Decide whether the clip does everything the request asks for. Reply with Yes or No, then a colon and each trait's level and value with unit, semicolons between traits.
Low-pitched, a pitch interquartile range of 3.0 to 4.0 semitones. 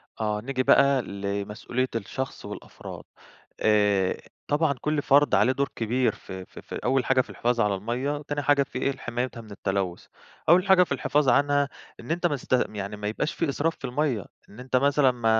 No: low, 130 Hz; average, 5.1 semitones